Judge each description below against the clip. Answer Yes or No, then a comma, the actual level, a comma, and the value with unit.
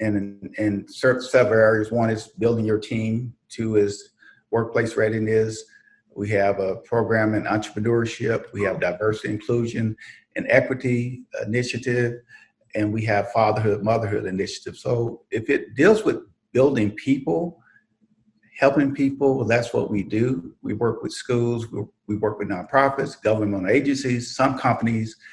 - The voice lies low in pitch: Yes, low, 115 Hz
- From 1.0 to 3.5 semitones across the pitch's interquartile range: Yes, narrow, 2.5 semitones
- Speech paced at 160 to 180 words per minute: No, average, 140 wpm